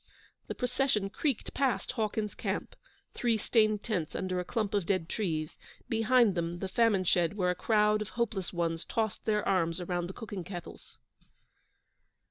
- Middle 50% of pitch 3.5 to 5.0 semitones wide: Yes, average, 3.9 semitones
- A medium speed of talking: Yes, average, 160 wpm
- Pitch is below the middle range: No, high, 205 Hz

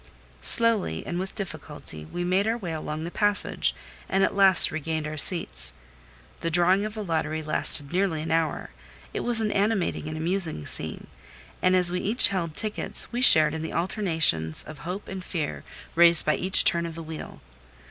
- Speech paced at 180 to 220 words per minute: Yes, average, 185 wpm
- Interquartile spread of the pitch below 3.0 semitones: No, average, 3.8 semitones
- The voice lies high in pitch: No, medium, 170 Hz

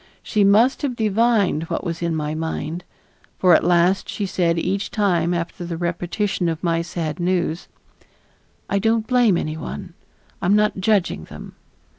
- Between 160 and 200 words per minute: Yes, average, 165 wpm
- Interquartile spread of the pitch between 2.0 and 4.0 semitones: Yes, average, 3.6 semitones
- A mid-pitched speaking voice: Yes, medium, 175 Hz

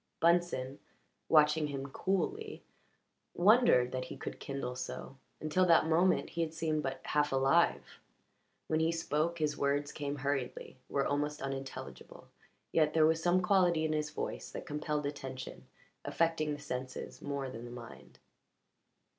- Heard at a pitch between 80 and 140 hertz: No, medium, 150 Hz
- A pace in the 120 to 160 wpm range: Yes, average, 145 wpm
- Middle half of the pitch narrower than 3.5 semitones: Yes, average, 3.1 semitones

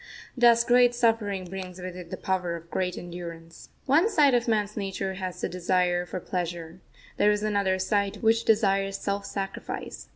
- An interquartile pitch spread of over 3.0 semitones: Yes, average, 3.4 semitones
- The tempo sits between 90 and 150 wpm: No, average, 170 wpm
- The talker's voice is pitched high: Yes, high, 195 Hz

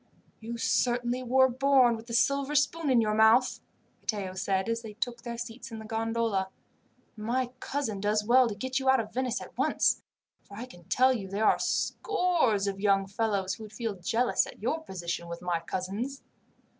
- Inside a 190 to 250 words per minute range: Yes, average, 195 wpm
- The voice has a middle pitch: No, high, 230 Hz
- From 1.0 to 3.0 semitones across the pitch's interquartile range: No, average, 3.9 semitones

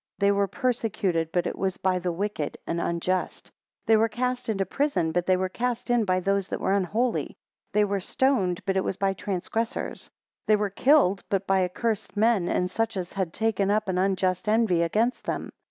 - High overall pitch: Yes, high, 195 Hz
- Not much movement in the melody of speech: No, average, 3.4 semitones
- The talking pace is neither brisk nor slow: No, fast, 215 wpm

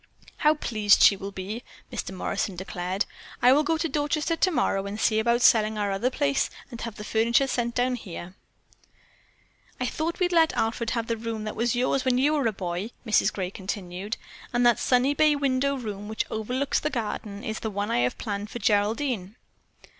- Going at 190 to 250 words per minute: Yes, average, 195 wpm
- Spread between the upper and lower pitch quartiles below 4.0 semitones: No, average, 4.3 semitones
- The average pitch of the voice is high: Yes, high, 230 Hz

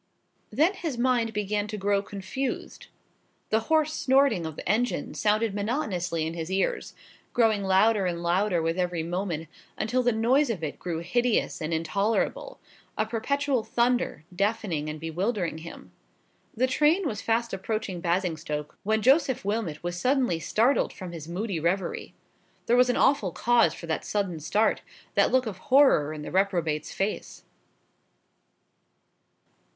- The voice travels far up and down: Yes, wide, 5.9 semitones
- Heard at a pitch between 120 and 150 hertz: No, high, 205 Hz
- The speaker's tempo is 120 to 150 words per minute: Yes, average, 145 wpm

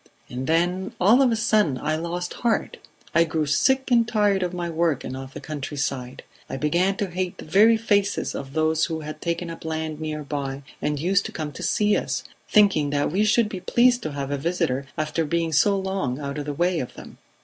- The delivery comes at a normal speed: No, fast, 220 wpm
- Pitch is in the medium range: Yes, medium, 165 Hz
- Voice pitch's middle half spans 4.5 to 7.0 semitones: Yes, average, 4.9 semitones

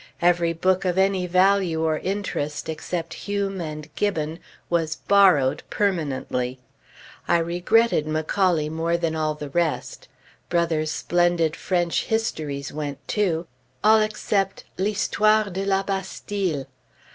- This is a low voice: No, medium, 175 Hz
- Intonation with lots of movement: No, average, 3.8 semitones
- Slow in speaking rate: Yes, slow, 120 wpm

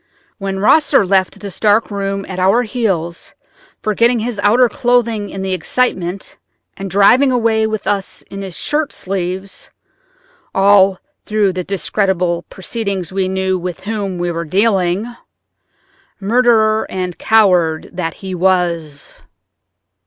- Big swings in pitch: No, average, 3.0 semitones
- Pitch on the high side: Yes, high, 195 Hz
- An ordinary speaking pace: No, slow, 125 wpm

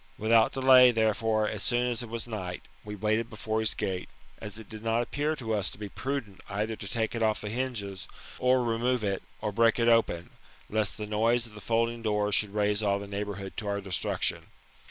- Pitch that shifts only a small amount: Yes, narrow, 2.1 semitones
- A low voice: Yes, low, 110 Hz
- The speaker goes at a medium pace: No, fast, 215 wpm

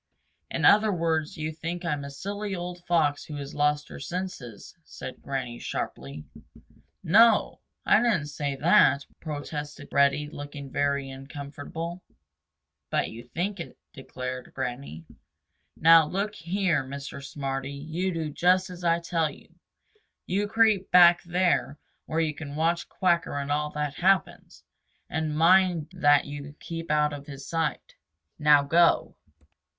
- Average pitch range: Yes, average, 3.6 semitones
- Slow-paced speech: No, average, 145 wpm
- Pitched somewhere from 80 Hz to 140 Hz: No, medium, 155 Hz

